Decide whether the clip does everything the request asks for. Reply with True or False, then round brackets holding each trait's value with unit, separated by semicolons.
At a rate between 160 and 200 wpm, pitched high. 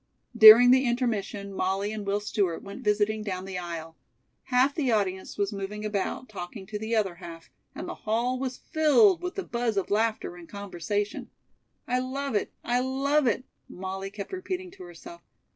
True (175 wpm; 215 Hz)